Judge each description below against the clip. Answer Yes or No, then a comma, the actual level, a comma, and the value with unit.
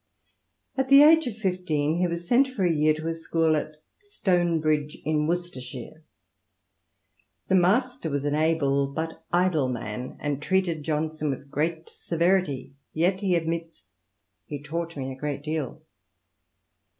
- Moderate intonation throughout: Yes, average, 3.4 semitones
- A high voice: No, medium, 160 Hz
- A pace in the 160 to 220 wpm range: No, average, 150 wpm